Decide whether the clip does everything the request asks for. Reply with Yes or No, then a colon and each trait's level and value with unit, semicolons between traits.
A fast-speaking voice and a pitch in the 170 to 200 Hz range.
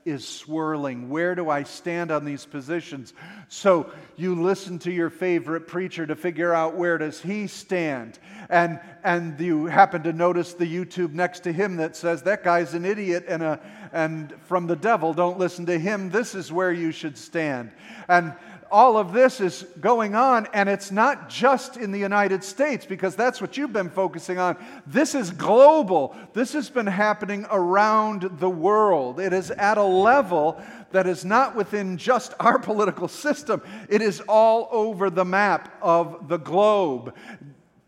No: average, 175 wpm; medium, 185 Hz